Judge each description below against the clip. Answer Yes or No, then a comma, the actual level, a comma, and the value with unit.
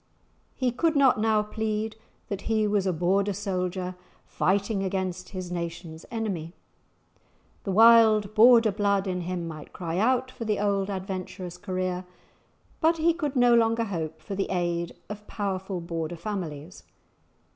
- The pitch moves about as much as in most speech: Yes, average, 3.5 semitones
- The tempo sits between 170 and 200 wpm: No, average, 145 wpm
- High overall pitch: Yes, high, 195 Hz